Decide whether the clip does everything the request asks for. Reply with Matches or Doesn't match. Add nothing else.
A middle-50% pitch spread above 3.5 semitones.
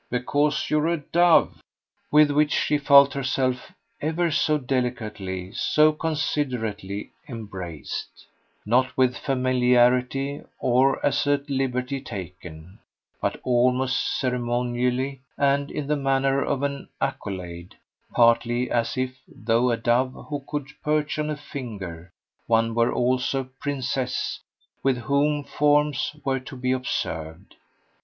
Doesn't match